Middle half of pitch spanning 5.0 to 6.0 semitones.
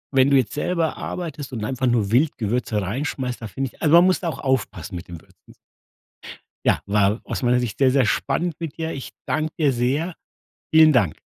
Yes: wide, 5.5 semitones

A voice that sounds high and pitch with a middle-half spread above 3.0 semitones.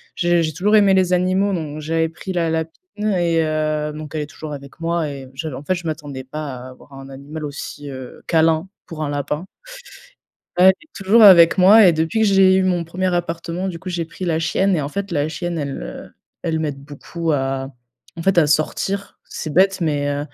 No: medium, 165 Hz; average, 3.6 semitones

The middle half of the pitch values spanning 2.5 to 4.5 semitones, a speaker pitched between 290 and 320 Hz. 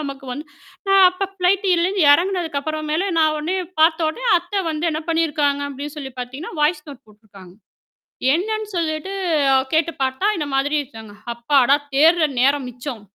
Yes: average, 3.7 semitones; very high, 305 Hz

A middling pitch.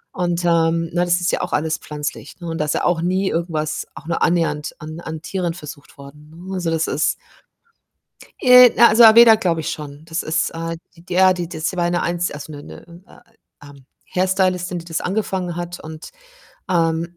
Yes: medium, 170 Hz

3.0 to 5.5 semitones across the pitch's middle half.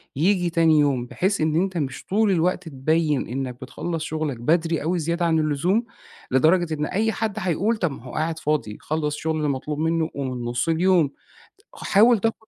Yes: average, 3.5 semitones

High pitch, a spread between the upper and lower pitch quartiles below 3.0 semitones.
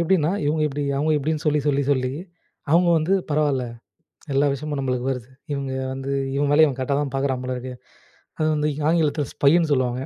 No: medium, 145 Hz; narrow, 2.5 semitones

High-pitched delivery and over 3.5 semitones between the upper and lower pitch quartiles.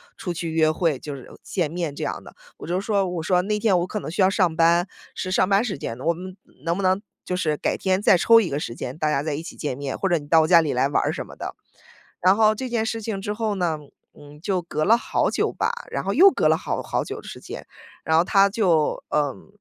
No: medium, 180 Hz; average, 4.1 semitones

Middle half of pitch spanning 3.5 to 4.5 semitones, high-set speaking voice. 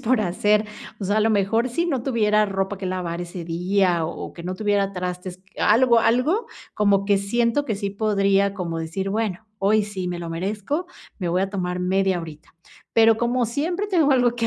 Yes: average, 3.9 semitones; high, 200 Hz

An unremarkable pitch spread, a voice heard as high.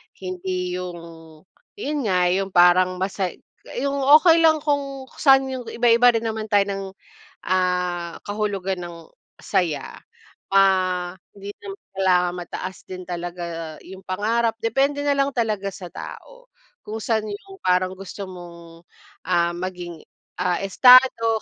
Yes: average, 4.5 semitones; high, 195 Hz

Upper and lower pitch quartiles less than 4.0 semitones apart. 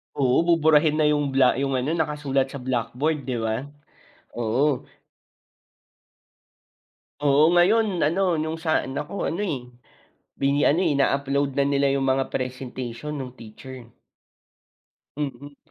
Yes: average, 2.9 semitones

